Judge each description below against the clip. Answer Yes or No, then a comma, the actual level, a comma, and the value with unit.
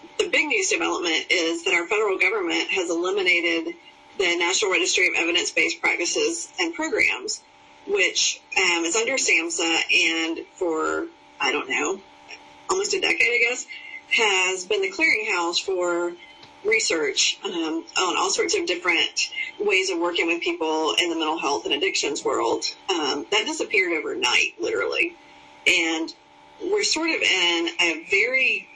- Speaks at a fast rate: No, average, 150 wpm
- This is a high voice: Yes, very high, 345 Hz